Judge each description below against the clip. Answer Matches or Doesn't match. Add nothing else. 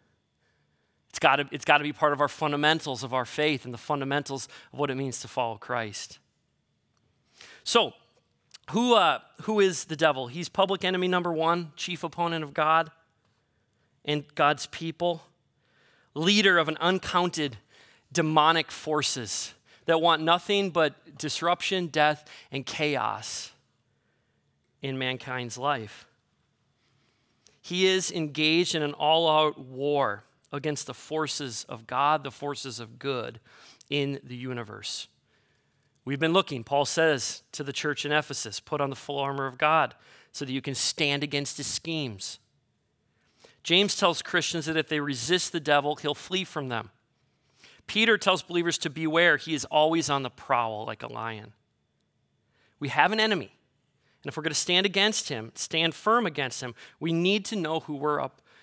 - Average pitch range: Matches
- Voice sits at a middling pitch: Matches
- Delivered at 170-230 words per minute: Doesn't match